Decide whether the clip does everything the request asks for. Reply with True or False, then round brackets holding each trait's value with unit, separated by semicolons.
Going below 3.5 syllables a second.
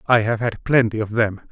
False (5.4 syllables/s)